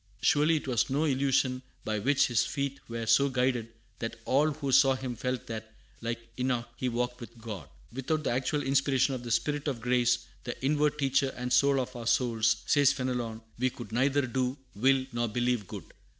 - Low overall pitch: Yes, low, 125 Hz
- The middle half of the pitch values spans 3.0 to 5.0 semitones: No, narrow, 2.6 semitones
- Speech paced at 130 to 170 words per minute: No, average, 195 wpm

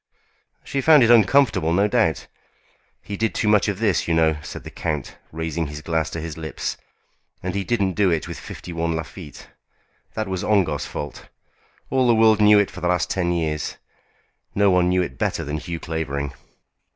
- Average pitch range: Yes, average, 4.4 semitones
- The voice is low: Yes, very low, 90 Hz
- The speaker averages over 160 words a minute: Yes, average, 190 wpm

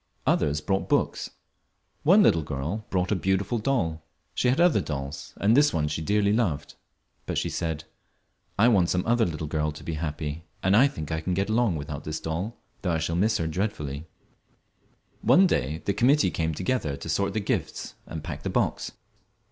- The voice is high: No, very low, 90 Hz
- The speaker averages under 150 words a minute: No, average, 190 wpm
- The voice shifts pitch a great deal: Yes, wide, 5.9 semitones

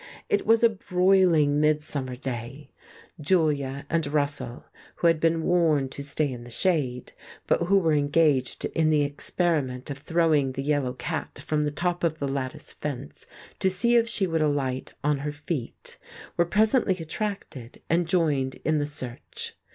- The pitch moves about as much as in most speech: Yes, average, 3.8 semitones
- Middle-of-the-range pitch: Yes, medium, 150 Hz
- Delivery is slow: No, average, 165 wpm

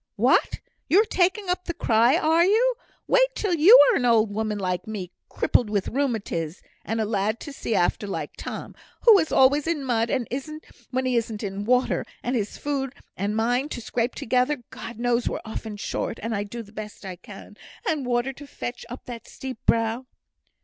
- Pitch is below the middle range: No, high, 240 Hz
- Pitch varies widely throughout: No, average, 4.9 semitones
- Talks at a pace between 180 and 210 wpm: Yes, average, 190 wpm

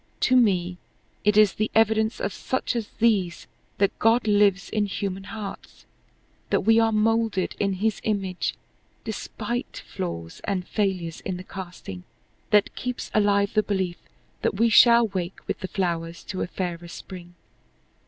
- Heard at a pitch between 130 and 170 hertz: No, high, 200 Hz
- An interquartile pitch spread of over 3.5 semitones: No, average, 3.2 semitones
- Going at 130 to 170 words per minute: Yes, average, 155 wpm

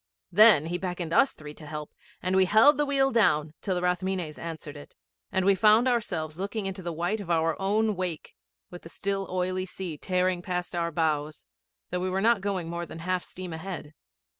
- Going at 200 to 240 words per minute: Yes, fast, 205 wpm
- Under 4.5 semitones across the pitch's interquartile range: Yes, average, 3.0 semitones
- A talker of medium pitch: Yes, medium, 180 Hz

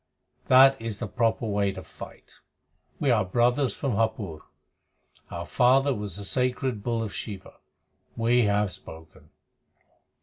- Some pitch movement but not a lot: Yes, average, 3.5 semitones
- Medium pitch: No, low, 115 Hz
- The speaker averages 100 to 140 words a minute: Yes, slow, 135 wpm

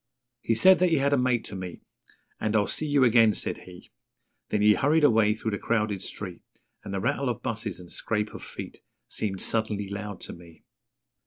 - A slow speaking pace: No, average, 200 wpm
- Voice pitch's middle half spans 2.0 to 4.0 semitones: Yes, average, 3.4 semitones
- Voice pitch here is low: Yes, low, 110 Hz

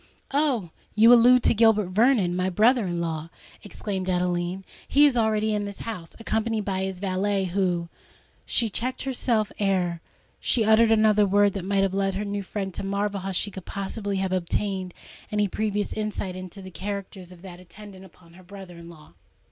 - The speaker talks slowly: No, average, 180 wpm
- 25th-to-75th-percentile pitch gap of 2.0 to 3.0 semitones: Yes, narrow, 2.6 semitones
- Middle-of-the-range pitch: No, high, 195 Hz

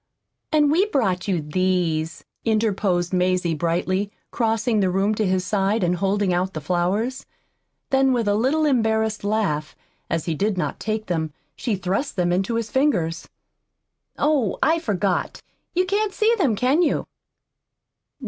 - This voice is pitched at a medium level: No, high, 205 Hz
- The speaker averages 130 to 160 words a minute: Yes, average, 150 wpm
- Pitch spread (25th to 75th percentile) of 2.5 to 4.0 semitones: No, average, 5.3 semitones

